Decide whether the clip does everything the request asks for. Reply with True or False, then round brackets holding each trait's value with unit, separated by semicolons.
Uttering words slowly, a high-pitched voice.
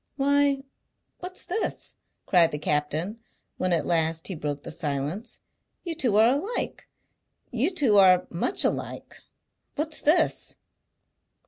True (125 wpm; 210 Hz)